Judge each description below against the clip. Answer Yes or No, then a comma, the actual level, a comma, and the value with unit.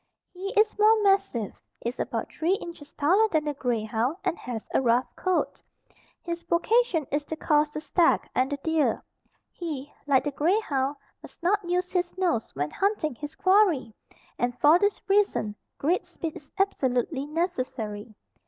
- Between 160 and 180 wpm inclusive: Yes, average, 165 wpm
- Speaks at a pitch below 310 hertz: No, very high, 315 Hz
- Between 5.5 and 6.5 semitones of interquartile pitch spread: Yes, wide, 5.9 semitones